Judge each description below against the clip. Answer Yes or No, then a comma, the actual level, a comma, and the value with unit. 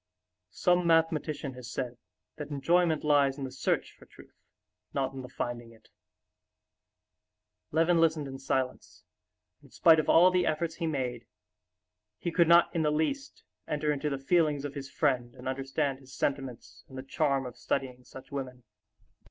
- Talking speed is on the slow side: No, average, 170 wpm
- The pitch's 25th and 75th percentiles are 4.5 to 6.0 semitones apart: No, average, 3.5 semitones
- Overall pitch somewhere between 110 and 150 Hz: Yes, medium, 140 Hz